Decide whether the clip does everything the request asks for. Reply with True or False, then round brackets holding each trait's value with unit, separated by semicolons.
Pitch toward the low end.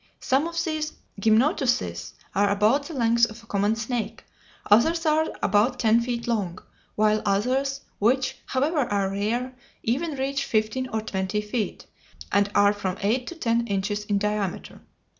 False (225 Hz)